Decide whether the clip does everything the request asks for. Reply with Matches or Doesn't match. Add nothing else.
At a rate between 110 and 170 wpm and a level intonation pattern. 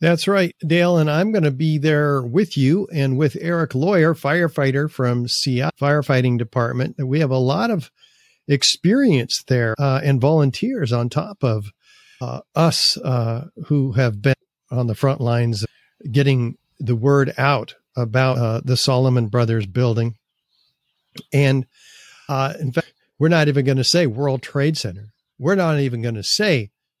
Doesn't match